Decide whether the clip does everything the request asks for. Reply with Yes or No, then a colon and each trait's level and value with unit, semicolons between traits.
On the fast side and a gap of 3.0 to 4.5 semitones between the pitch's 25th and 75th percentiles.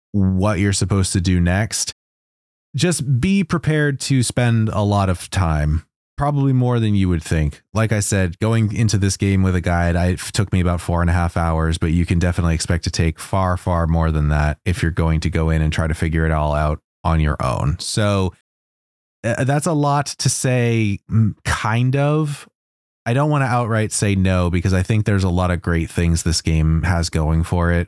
No: fast, 215 wpm; average, 5.0 semitones